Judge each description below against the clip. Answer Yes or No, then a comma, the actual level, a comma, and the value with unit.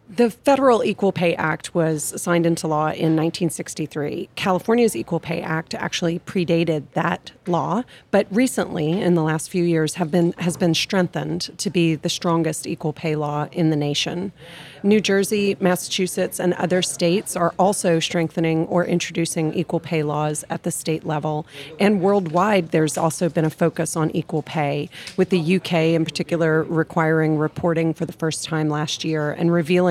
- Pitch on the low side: No, medium, 170 Hz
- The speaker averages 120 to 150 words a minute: No, average, 170 wpm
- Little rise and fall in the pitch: Yes, narrow, 2.3 semitones